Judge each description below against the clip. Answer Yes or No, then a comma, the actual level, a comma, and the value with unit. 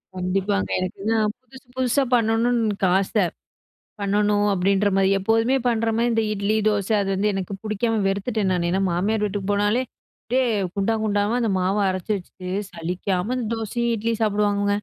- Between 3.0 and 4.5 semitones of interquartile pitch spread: No, narrow, 2.6 semitones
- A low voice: No, high, 205 Hz